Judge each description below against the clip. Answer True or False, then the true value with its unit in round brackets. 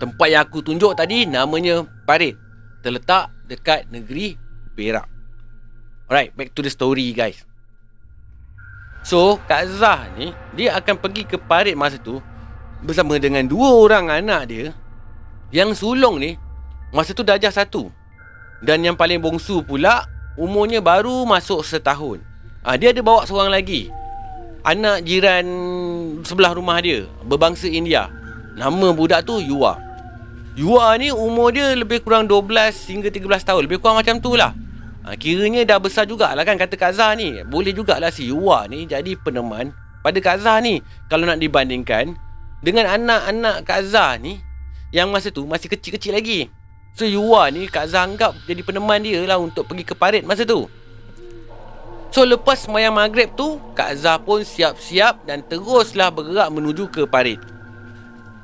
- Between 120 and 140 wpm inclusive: False (150 wpm)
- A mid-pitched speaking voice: True (170 Hz)